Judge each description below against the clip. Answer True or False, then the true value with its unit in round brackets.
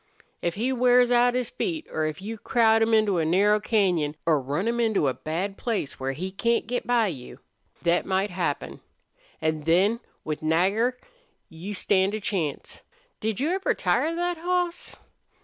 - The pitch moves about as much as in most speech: False (6.2 semitones)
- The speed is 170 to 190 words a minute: True (175 wpm)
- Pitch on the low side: False (205 Hz)